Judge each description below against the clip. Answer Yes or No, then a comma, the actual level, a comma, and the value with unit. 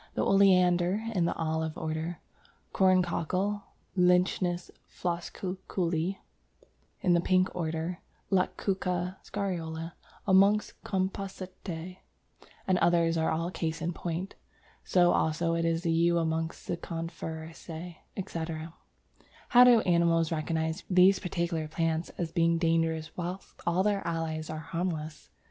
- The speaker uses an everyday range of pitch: No, narrow, 2.1 semitones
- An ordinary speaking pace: No, slow, 115 wpm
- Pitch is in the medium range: Yes, medium, 170 Hz